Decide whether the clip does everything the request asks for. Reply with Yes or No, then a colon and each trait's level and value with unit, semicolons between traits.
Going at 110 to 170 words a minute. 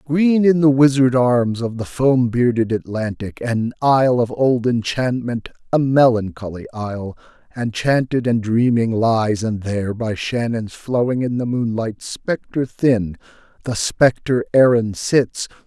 Yes: average, 140 wpm